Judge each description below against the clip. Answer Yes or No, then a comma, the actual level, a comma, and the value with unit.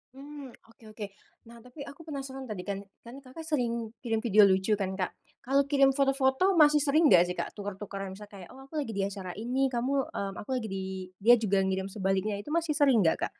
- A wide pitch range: Yes, wide, 5.7 semitones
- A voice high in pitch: Yes, high, 235 Hz